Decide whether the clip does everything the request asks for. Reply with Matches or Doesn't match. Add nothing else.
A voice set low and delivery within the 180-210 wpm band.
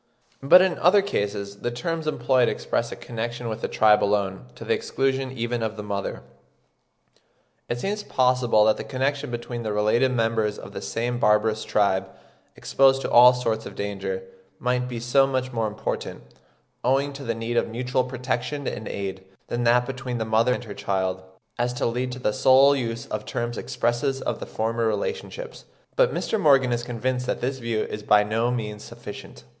Matches